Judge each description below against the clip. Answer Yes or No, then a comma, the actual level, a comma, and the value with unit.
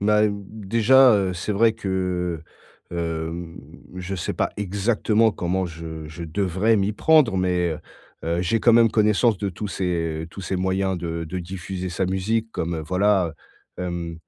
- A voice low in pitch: Yes, very low, 95 Hz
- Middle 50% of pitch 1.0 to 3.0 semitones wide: No, average, 3.4 semitones